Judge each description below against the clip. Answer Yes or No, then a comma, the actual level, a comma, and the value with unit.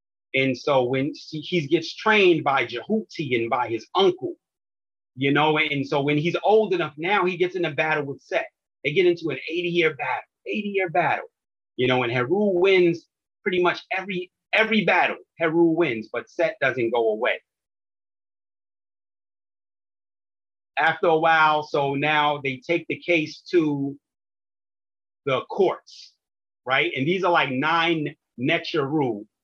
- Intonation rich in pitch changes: Yes, wide, 7.1 semitones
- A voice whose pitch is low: No, medium, 150 Hz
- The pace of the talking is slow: No, average, 145 wpm